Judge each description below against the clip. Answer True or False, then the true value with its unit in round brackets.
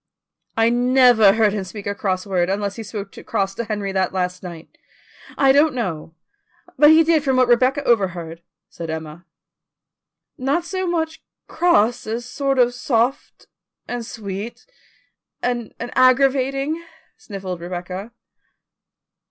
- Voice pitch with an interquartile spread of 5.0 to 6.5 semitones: True (5.6 semitones)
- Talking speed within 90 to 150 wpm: True (135 wpm)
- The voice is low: False (230 Hz)